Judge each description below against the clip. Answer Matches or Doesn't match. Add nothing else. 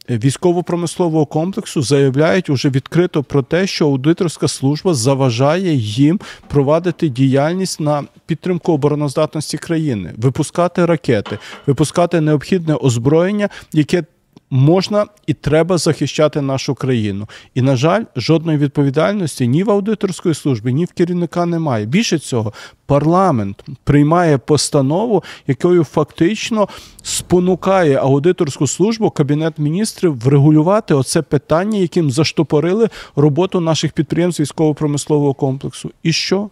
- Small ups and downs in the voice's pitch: Doesn't match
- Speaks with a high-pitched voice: Doesn't match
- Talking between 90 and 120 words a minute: Matches